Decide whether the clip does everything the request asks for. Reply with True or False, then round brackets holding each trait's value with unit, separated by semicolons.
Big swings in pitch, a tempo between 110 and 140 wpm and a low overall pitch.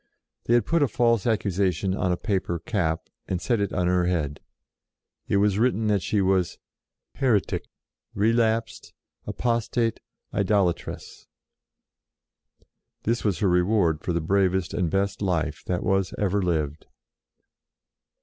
False (3.7 semitones; 135 wpm; 95 Hz)